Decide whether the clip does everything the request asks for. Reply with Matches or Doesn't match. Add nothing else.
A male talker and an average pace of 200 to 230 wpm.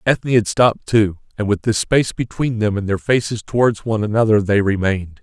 Matches